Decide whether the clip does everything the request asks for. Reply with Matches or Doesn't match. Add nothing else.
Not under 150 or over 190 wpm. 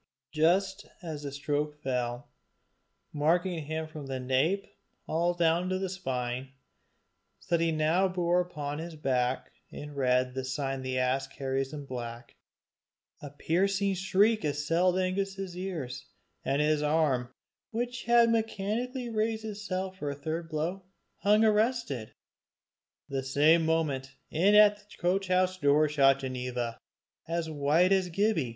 Doesn't match